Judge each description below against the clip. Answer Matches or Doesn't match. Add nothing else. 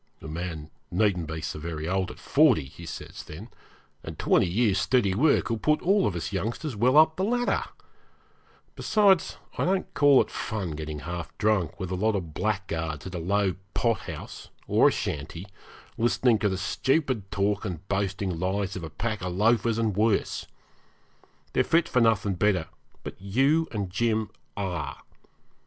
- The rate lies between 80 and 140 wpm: Doesn't match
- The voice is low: Matches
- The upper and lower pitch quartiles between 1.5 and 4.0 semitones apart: Doesn't match